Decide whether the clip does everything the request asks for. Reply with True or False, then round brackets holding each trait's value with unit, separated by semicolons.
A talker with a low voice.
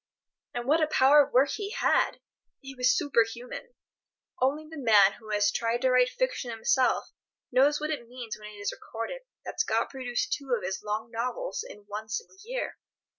False (250 Hz)